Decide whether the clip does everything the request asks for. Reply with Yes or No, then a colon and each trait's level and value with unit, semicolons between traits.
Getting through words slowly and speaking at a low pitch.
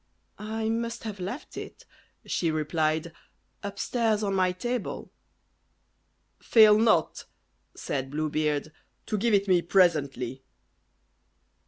No: slow, 110 wpm; medium, 185 Hz